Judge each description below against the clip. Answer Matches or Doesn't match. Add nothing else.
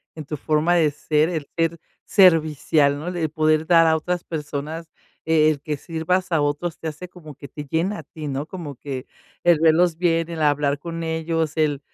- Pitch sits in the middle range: Matches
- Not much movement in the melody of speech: Matches